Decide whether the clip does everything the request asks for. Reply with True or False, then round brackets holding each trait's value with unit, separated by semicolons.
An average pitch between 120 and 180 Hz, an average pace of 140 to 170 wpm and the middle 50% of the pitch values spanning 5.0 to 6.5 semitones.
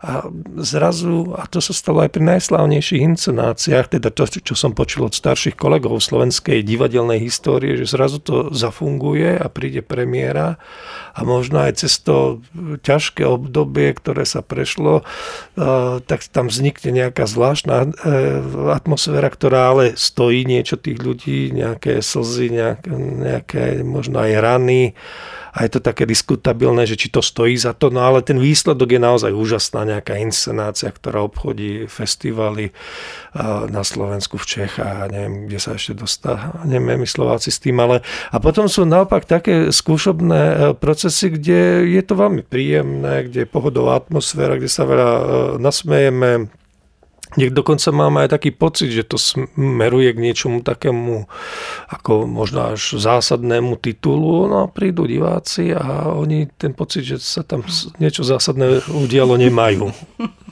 True (130 Hz; 145 wpm; 5.5 semitones)